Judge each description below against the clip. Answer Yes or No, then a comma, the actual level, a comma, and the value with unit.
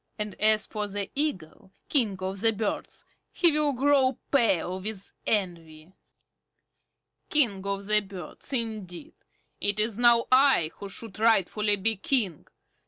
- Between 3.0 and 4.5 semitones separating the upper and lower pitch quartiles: Yes, average, 3.8 semitones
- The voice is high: Yes, high, 210 Hz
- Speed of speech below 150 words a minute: Yes, slow, 135 wpm